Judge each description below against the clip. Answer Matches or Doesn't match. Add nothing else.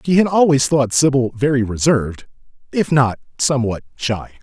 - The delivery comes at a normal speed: Matches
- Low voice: Matches